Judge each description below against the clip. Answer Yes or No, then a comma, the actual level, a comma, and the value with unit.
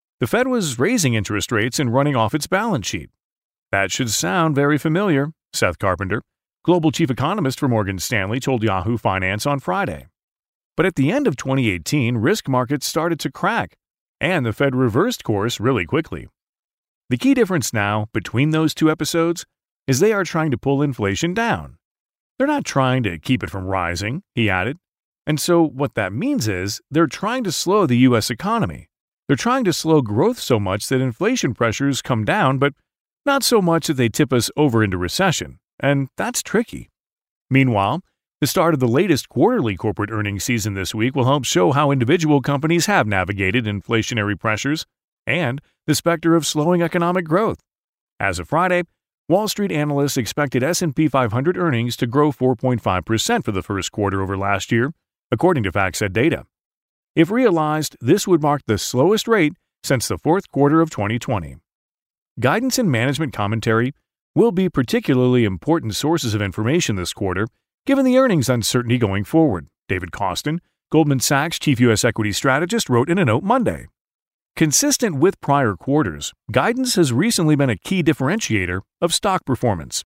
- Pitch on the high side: No, low, 135 Hz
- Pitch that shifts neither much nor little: No, wide, 6.6 semitones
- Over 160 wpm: Yes, average, 170 wpm